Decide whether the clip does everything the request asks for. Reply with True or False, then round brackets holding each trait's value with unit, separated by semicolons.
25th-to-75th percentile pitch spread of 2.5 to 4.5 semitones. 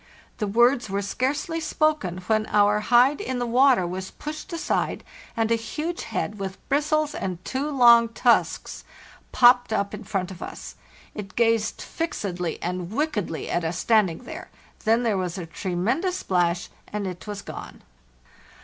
False (5.5 semitones)